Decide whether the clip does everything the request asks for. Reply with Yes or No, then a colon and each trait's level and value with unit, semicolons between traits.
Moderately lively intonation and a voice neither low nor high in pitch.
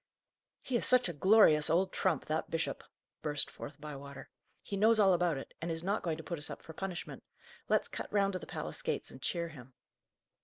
Yes: average, 4.2 semitones; medium, 170 Hz